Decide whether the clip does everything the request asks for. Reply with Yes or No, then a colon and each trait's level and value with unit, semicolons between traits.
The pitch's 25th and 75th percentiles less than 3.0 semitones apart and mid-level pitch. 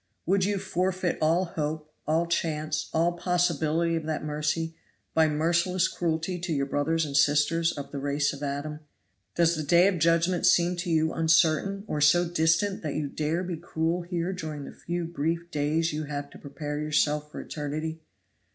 Yes: narrow, 2.4 semitones; medium, 160 Hz